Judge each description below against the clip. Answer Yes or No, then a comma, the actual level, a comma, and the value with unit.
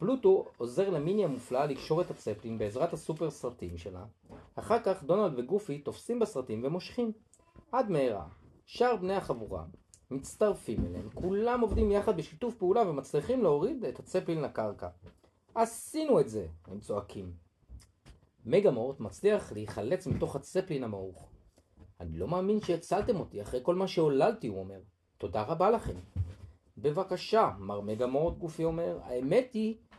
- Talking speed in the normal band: Yes, average, 140 wpm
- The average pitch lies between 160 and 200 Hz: No, medium, 140 Hz